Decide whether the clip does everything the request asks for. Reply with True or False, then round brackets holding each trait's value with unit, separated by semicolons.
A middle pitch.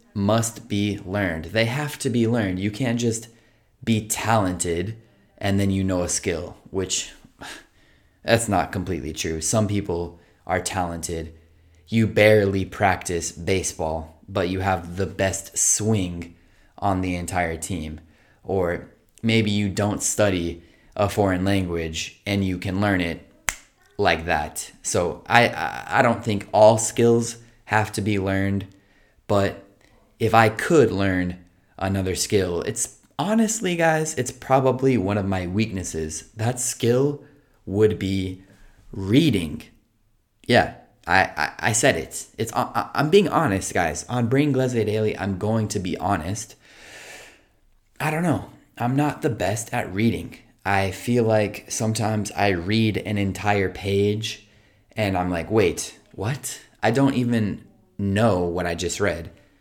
False (100 Hz)